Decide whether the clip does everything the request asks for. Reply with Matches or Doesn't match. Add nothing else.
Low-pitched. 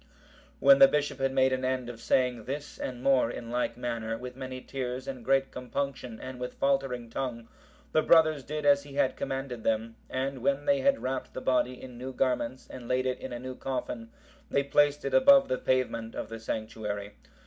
Matches